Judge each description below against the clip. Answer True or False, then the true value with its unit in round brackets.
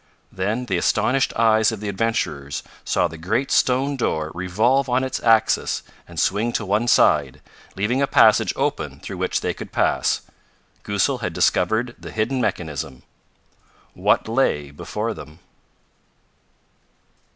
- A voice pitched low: True (110 Hz)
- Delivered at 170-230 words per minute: False (140 wpm)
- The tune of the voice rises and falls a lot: True (5.8 semitones)